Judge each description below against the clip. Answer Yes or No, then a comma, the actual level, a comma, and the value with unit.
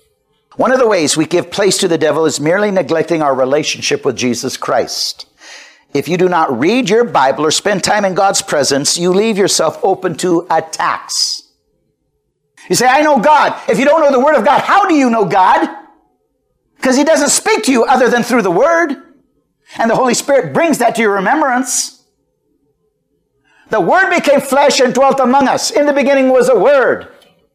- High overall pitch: Yes, high, 240 Hz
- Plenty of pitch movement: Yes, wide, 7.8 semitones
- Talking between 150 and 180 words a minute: No, average, 195 wpm